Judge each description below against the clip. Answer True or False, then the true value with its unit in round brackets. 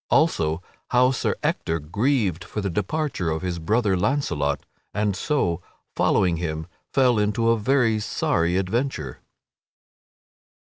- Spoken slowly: True (125 wpm)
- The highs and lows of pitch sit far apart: True (6.6 semitones)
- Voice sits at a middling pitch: False (100 Hz)